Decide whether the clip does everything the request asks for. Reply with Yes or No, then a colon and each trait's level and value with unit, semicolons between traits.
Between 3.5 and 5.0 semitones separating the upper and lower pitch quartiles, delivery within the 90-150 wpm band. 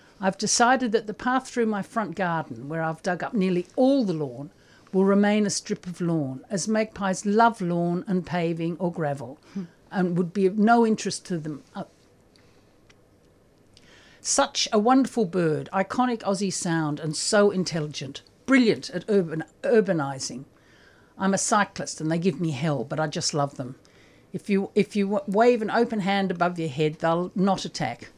No: average, 4.7 semitones; average, 170 wpm